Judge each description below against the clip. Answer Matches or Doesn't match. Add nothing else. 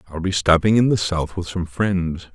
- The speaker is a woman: Doesn't match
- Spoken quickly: Matches